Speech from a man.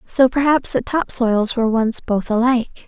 No: female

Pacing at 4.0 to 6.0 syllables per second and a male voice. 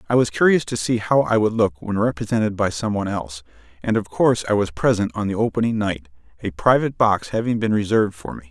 No: 6.4 syllables/s; male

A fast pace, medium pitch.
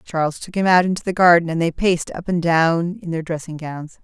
Yes: fast, 255 wpm; medium, 170 Hz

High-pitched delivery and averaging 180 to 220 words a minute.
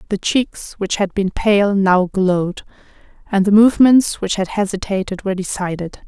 No: high, 195 Hz; average, 160 wpm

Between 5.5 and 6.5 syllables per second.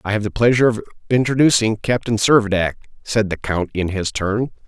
Yes: 5.7 syllables/s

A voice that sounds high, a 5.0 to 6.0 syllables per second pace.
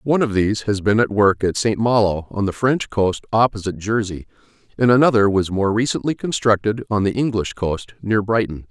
No: low, 105 Hz; 5.4 syllables/s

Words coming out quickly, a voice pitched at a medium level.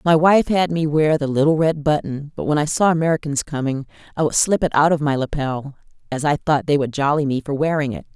Yes: fast, 245 wpm; medium, 150 Hz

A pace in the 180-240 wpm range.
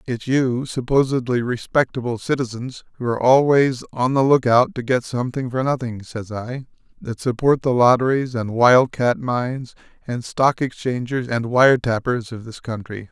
No: average, 160 wpm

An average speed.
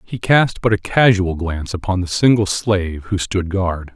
Yes: average, 195 wpm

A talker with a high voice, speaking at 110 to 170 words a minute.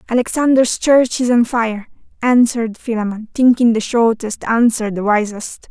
Yes: high, 230 Hz; slow, 135 wpm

